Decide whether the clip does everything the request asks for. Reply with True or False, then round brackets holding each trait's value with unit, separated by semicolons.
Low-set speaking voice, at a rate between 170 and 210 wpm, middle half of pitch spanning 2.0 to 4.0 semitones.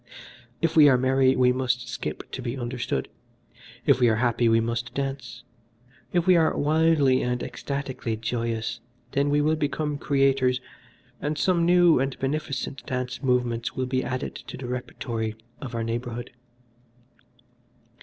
False (130 Hz; 150 wpm; 2.8 semitones)